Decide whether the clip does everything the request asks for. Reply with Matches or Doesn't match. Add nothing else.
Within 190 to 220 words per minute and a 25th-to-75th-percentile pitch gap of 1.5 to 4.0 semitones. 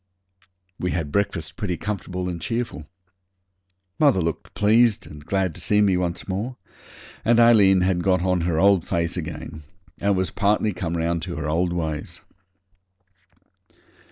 Doesn't match